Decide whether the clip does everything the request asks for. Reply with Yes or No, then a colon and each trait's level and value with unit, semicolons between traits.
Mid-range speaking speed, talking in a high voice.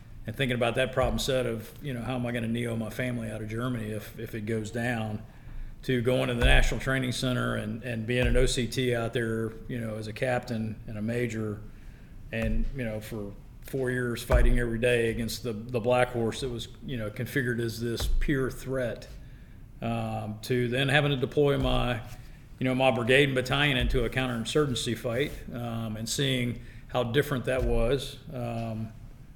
No: average, 195 wpm; low, 120 Hz